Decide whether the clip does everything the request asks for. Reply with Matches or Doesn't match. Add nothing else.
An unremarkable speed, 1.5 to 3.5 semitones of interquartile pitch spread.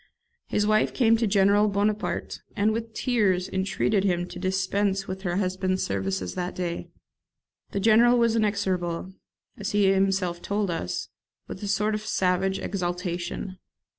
Matches